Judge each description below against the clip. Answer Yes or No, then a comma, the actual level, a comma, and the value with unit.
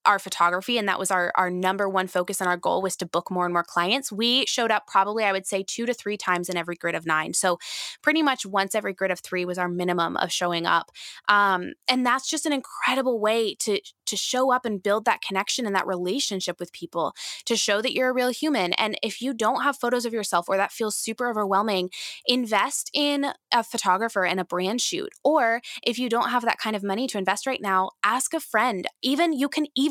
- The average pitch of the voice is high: Yes, high, 205 Hz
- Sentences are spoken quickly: Yes, fast, 235 wpm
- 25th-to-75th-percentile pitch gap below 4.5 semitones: No, average, 5.1 semitones